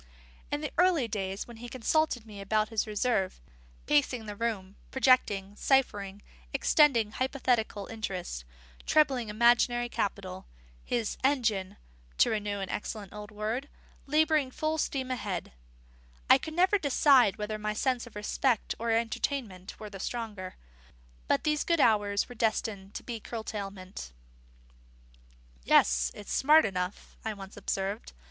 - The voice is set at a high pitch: Yes, high, 220 Hz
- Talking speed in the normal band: No, slow, 130 wpm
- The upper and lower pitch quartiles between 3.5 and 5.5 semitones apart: Yes, average, 4.2 semitones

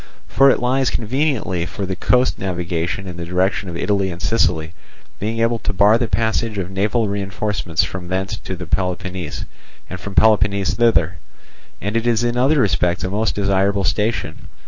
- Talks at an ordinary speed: Yes, average, 170 wpm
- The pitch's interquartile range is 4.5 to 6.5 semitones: No, average, 3.7 semitones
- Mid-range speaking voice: No, low, 100 Hz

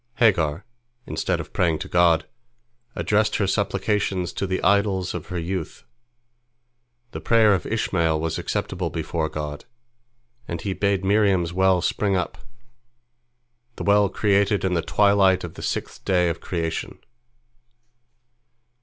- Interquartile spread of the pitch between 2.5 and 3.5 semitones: Yes, average, 3.1 semitones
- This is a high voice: No, very low, 95 Hz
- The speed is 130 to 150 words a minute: Yes, slow, 135 wpm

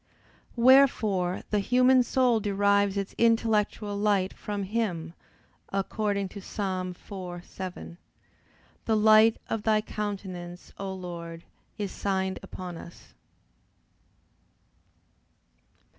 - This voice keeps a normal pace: No, slow, 95 wpm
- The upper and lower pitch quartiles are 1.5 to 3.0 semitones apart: Yes, average, 2.7 semitones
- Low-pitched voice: No, high, 200 Hz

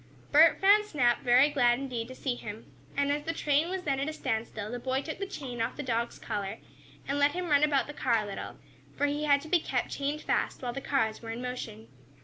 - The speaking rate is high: Yes, fast, 245 wpm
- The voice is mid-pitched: No, very high, 275 Hz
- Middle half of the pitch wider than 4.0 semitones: No, average, 3.6 semitones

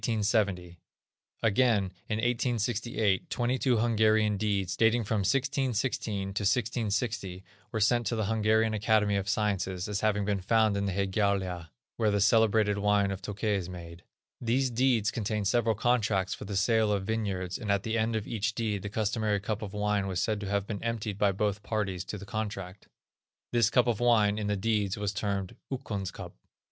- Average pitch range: No, narrow, 2.2 semitones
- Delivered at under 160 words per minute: No, average, 175 wpm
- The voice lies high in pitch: No, low, 105 Hz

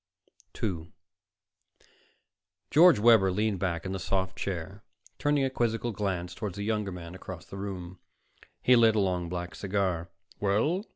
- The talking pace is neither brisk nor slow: Yes, average, 150 wpm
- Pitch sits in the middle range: No, very low, 95 Hz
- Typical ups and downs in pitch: Yes, average, 3.4 semitones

